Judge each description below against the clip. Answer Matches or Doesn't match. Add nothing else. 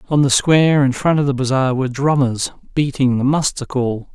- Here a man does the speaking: Matches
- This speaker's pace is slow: Doesn't match